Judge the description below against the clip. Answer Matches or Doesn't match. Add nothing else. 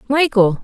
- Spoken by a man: Doesn't match